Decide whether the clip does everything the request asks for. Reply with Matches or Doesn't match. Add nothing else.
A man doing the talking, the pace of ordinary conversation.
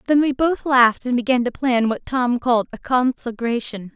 Doesn't match